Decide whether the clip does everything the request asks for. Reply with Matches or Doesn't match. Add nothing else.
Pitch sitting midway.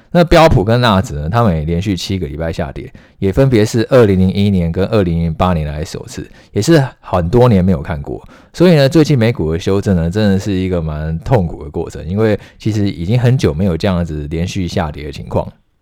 Doesn't match